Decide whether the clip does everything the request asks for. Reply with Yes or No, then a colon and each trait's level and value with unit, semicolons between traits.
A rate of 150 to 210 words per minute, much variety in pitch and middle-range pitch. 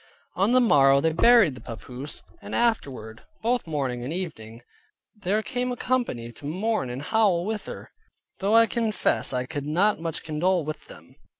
Yes: average, 175 wpm; wide, 8.3 semitones; medium, 170 Hz